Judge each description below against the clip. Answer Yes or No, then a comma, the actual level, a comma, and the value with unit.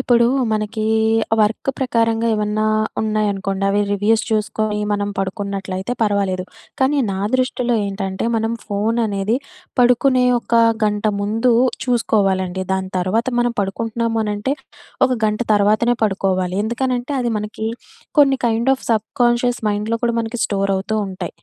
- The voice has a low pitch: No, high, 215 Hz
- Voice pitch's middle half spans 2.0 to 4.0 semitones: Yes, average, 2.9 semitones